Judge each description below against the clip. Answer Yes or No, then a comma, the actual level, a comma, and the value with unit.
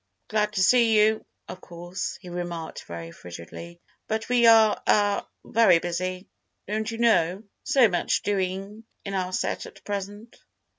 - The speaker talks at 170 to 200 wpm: No, average, 140 wpm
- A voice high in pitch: Yes, high, 200 Hz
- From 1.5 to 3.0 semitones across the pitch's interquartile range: No, average, 3.7 semitones